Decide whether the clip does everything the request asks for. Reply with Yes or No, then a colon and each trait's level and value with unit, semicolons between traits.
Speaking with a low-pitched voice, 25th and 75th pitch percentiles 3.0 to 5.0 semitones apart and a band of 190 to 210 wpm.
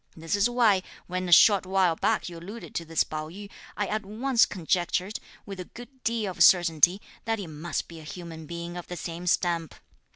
No: medium, 180 Hz; average, 3.4 semitones; fast, 205 wpm